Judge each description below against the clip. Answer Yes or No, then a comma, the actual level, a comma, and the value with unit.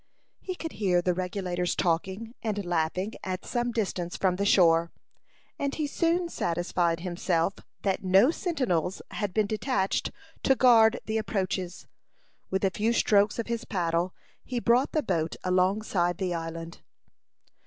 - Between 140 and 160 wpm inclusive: Yes, average, 145 wpm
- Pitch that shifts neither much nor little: Yes, average, 4.3 semitones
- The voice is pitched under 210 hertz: Yes, high, 190 Hz